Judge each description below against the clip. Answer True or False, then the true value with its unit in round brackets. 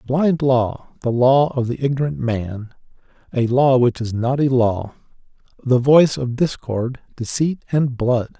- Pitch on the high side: False (125 Hz)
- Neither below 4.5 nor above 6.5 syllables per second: False (4.0 syllables/s)